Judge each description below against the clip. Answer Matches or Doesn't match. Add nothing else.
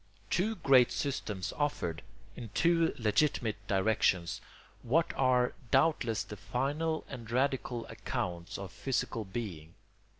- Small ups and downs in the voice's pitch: Doesn't match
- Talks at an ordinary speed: Doesn't match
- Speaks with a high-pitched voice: Doesn't match